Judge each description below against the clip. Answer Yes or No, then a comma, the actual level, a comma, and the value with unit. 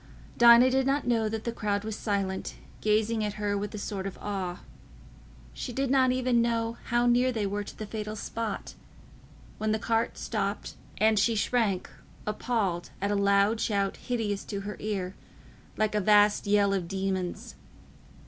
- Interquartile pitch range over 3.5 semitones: No, narrow, 2.5 semitones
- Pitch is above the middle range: Yes, high, 210 Hz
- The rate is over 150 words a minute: Yes, average, 165 wpm